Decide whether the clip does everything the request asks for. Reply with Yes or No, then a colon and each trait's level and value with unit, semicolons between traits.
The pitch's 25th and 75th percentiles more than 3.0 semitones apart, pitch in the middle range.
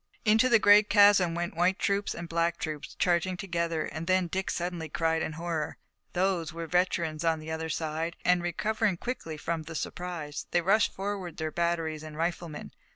No: narrow, 2.5 semitones; medium, 170 Hz